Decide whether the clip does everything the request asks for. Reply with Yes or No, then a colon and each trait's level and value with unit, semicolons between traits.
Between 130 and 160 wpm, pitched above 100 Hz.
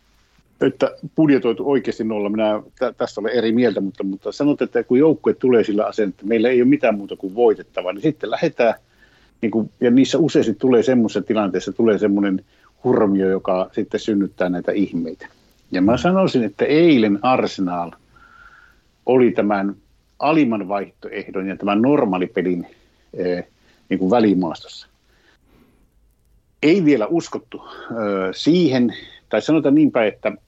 Yes: average, 135 wpm; low, 110 Hz